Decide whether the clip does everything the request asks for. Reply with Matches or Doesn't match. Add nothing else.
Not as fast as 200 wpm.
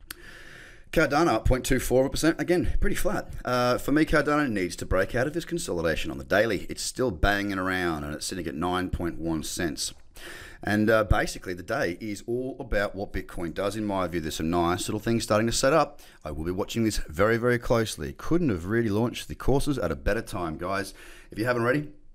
Doesn't match